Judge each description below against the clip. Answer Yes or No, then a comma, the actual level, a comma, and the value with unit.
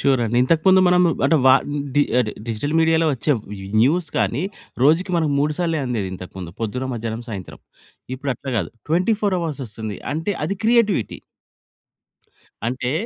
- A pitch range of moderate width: No, wide, 6.4 semitones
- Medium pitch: Yes, medium, 145 Hz